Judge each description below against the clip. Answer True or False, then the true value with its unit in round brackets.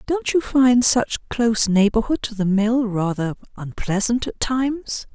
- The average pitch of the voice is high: True (230 Hz)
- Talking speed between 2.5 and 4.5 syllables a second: True (4.3 syllables/s)